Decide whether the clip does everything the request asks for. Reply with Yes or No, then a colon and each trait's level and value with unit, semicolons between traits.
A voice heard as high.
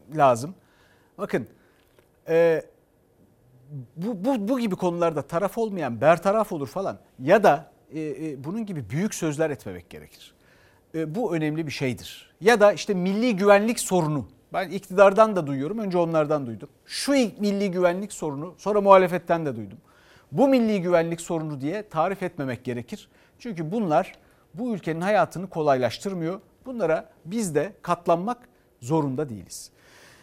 No: medium, 170 Hz